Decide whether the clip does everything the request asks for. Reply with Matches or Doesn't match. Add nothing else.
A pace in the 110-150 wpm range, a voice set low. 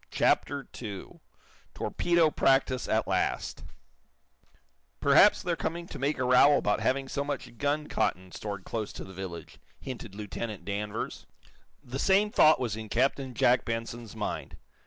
Matches